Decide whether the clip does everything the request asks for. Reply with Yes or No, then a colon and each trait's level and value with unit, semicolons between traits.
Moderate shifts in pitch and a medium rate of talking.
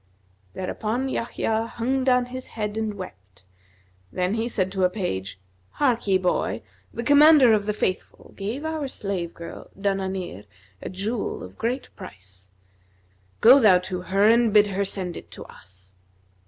Yes: average, 4.5 semitones; average, 155 wpm